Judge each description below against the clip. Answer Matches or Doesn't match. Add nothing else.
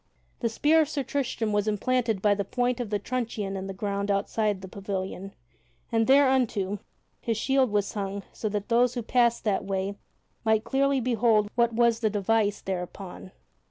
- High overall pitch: Matches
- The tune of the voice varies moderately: Matches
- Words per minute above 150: Matches